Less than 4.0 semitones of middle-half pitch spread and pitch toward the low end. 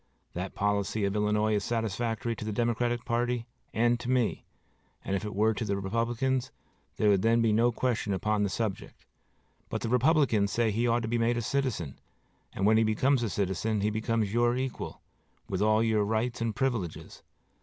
Yes: narrow, 2.4 semitones; low, 110 Hz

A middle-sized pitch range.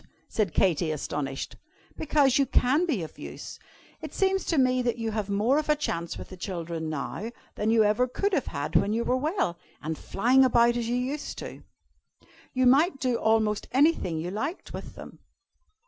No: wide, 6.5 semitones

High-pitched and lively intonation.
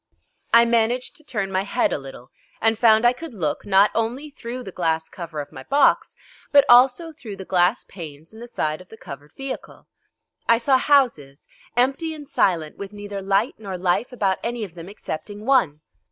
Yes: high, 210 Hz; wide, 5.9 semitones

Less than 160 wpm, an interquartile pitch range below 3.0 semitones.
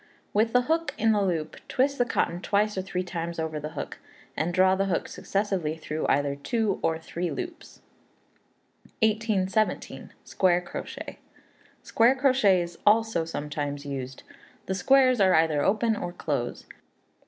No: average, 150 wpm; wide, 5.4 semitones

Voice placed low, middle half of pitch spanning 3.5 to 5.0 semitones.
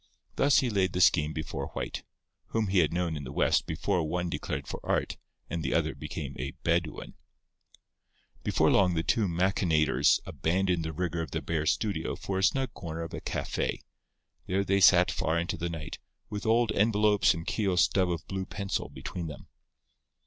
No: very low, 90 Hz; average, 3.1 semitones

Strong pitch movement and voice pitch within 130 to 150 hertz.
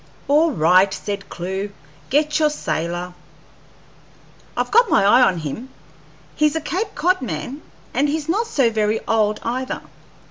No: wide, 8.0 semitones; high, 245 Hz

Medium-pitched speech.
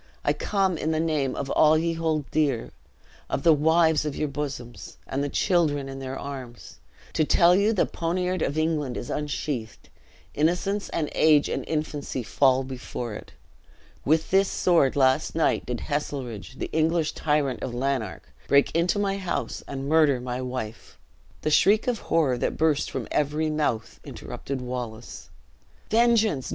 Yes: medium, 150 Hz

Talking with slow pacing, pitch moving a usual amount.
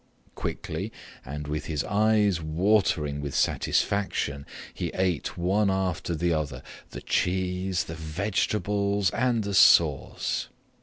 Yes: slow, 115 wpm; average, 4.5 semitones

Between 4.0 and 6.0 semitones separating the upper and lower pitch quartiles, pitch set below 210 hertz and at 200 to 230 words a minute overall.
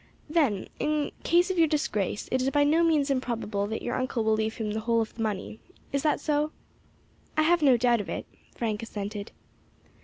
No: wide, 5.5 semitones; high, 245 Hz; fast, 205 wpm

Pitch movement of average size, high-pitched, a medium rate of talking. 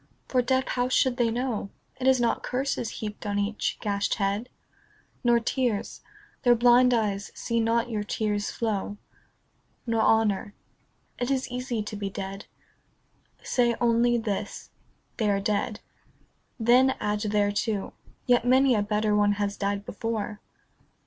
Yes: average, 3.0 semitones; high, 225 Hz; average, 150 wpm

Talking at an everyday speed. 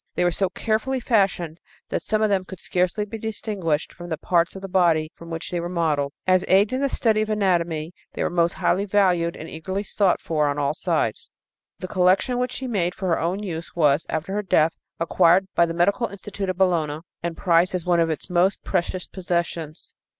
No: fast, 215 wpm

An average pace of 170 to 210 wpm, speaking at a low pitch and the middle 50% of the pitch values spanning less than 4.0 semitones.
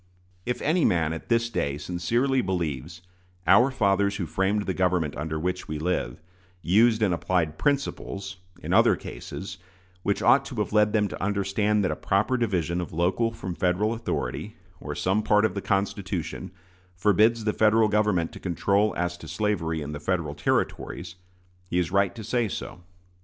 Yes: average, 175 wpm; very low, 95 Hz; average, 3.6 semitones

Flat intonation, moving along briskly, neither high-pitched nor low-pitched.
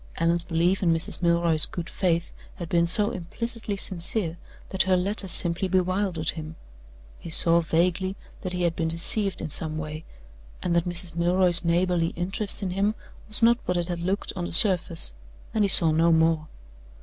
No: narrow, 2.1 semitones; average, 180 wpm; medium, 175 Hz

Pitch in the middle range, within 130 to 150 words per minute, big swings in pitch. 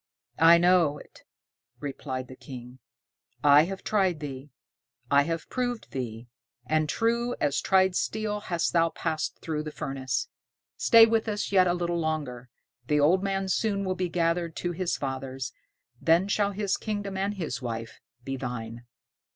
No: medium, 165 Hz; average, 160 wpm; wide, 6.1 semitones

